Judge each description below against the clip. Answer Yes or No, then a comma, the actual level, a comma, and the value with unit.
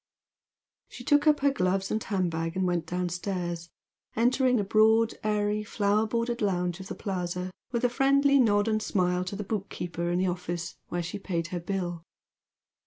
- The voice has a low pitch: No, high, 195 Hz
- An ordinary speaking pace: Yes, average, 180 wpm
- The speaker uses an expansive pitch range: No, average, 3.8 semitones